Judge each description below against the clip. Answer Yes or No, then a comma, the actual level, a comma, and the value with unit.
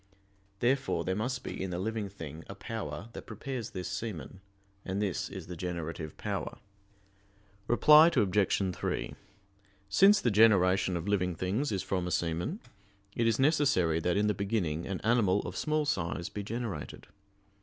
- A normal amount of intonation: Yes, average, 4.4 semitones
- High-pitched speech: No, low, 100 Hz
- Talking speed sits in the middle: Yes, average, 160 wpm